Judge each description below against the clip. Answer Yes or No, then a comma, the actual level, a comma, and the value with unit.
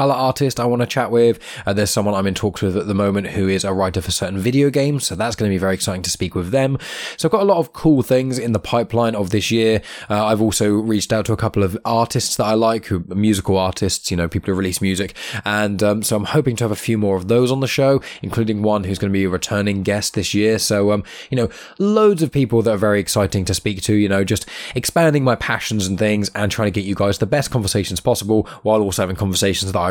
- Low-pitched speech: Yes, low, 105 Hz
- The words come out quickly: Yes, fast, 275 wpm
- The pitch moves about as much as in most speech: Yes, average, 3.1 semitones